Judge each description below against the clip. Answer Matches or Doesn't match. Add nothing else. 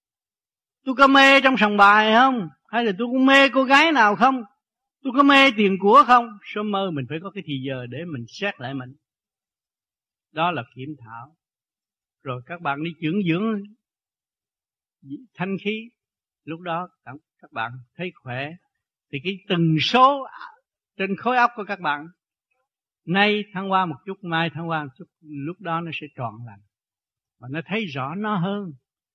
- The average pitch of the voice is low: Doesn't match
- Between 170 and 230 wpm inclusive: Matches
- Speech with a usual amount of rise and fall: Doesn't match